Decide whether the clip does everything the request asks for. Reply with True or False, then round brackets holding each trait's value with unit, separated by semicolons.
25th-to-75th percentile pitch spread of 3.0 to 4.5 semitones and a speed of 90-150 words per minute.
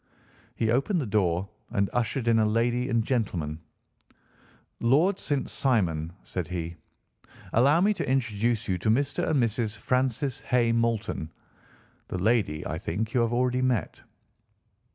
True (4.2 semitones; 145 wpm)